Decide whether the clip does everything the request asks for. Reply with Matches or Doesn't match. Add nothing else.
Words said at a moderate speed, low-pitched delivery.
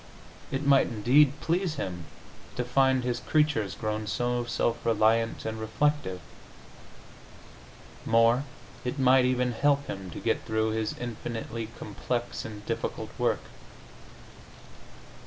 Doesn't match